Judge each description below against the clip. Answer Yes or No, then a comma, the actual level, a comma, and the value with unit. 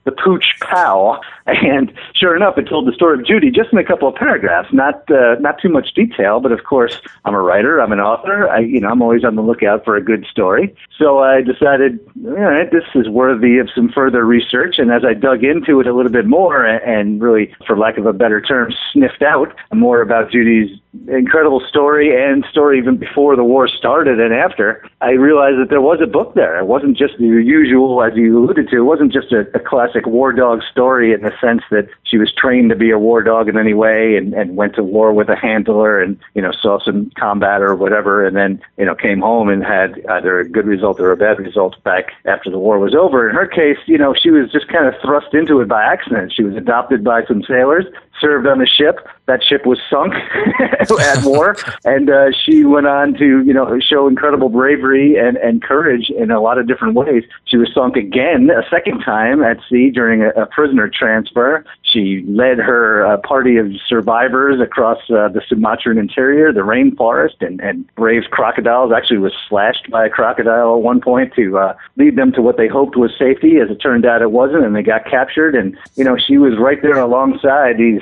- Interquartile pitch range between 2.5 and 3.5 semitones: No, average, 4.0 semitones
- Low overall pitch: Yes, low, 125 Hz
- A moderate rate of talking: No, fast, 220 wpm